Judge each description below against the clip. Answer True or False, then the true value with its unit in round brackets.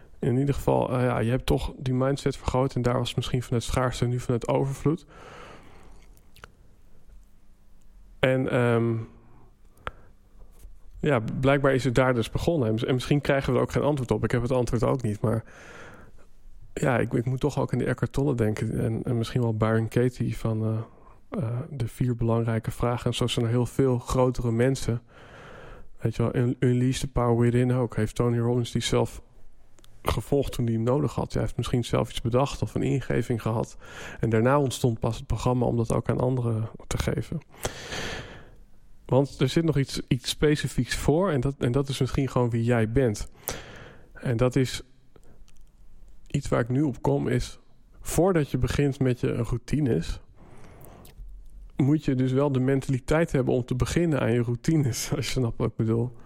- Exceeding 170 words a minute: True (185 wpm)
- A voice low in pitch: True (125 Hz)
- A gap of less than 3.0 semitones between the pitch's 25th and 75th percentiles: True (2.6 semitones)